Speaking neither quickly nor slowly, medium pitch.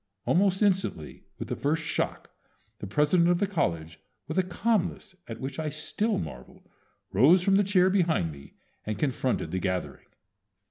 Yes: average, 165 wpm; medium, 160 Hz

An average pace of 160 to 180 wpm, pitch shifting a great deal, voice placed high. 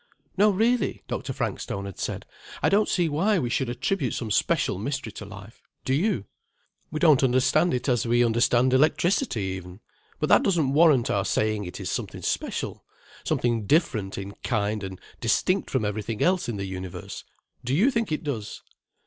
No: average, 170 wpm; wide, 7.2 semitones; low, 125 Hz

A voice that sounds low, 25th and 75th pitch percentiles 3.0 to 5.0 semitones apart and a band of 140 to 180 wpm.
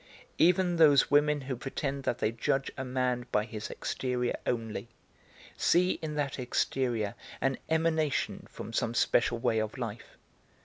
Yes: low, 130 Hz; average, 4.0 semitones; average, 145 wpm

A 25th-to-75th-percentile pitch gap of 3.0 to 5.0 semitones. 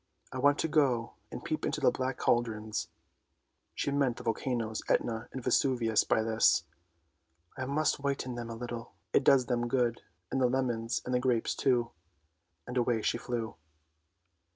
No: narrow, 2.4 semitones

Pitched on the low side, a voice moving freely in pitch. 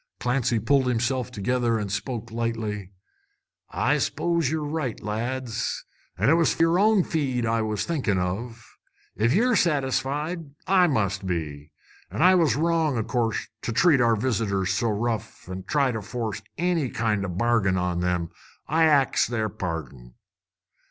Yes: low, 120 Hz; wide, 5.9 semitones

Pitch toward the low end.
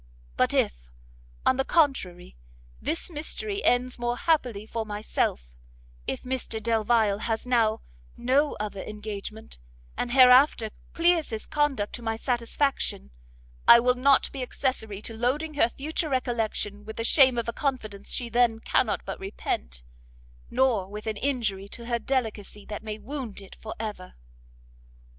No: high, 235 Hz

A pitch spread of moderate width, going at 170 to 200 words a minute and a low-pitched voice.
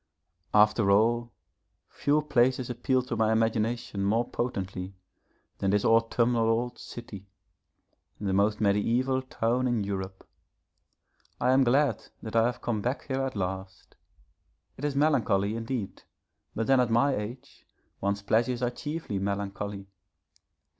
No: average, 3.7 semitones; slow, 135 wpm; low, 115 Hz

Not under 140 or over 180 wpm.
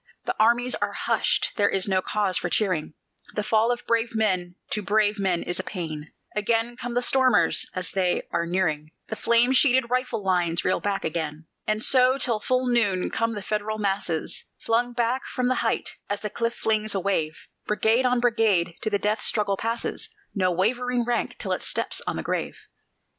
No: average, 195 wpm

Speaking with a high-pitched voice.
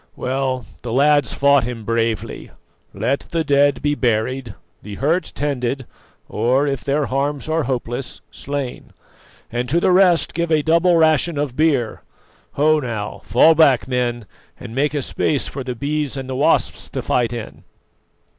No: low, 135 Hz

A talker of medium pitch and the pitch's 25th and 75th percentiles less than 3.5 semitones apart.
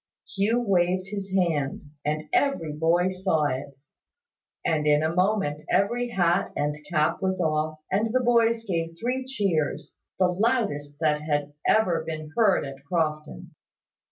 No: medium, 170 Hz; average, 4.8 semitones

